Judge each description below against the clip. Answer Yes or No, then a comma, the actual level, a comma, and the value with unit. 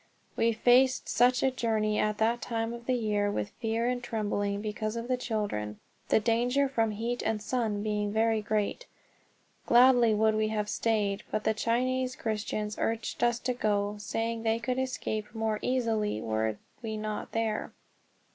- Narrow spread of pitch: Yes, narrow, 2.1 semitones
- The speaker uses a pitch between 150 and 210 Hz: No, high, 220 Hz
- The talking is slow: No, average, 165 wpm